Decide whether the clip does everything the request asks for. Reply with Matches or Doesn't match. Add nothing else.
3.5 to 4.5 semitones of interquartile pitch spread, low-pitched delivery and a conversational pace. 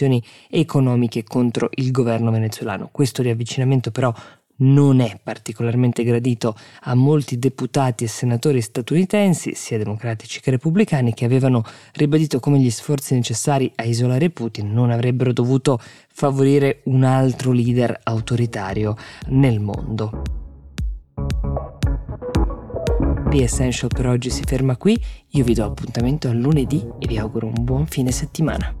Doesn't match